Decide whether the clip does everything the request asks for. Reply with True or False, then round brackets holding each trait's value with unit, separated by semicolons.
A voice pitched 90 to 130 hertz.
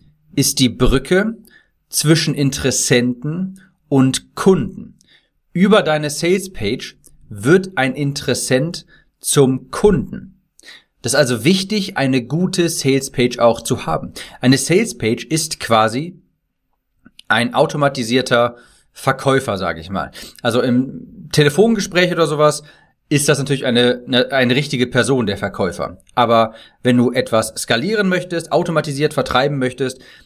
False (140 Hz)